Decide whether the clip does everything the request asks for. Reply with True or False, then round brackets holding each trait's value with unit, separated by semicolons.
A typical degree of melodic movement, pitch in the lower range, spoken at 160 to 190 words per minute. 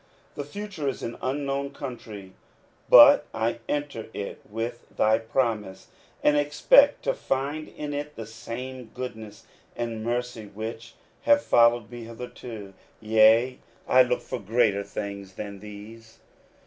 False (3.6 semitones; 115 Hz; 135 wpm)